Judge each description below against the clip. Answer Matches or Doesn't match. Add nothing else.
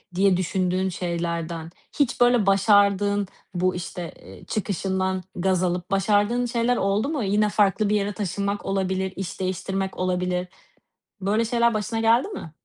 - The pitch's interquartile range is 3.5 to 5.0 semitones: Doesn't match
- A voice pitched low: Doesn't match